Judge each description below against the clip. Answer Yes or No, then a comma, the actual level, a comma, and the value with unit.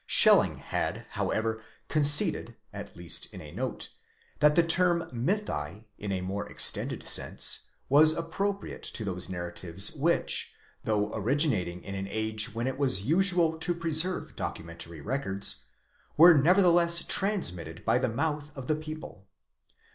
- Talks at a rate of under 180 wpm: Yes, average, 140 wpm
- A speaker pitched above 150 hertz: No, low, 135 Hz